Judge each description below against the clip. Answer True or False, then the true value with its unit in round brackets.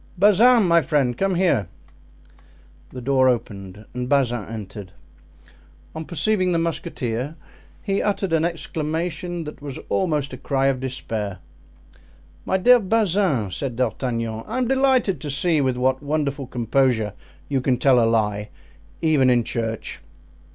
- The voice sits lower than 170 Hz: True (140 Hz)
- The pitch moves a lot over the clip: True (6.1 semitones)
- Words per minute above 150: False (140 wpm)